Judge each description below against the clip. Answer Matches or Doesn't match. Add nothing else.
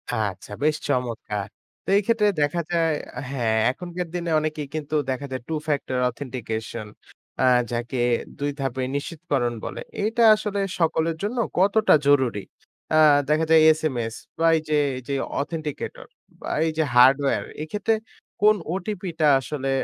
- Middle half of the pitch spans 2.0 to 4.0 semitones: Doesn't match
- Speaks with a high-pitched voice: Doesn't match